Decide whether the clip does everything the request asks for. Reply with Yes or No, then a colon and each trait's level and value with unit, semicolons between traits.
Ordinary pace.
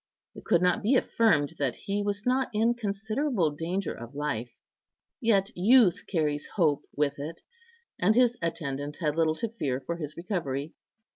Yes: average, 160 wpm